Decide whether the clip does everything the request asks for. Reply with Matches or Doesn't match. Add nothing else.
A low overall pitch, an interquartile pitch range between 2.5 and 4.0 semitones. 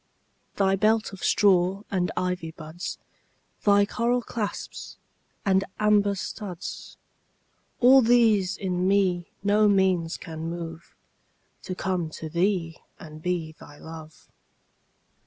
Doesn't match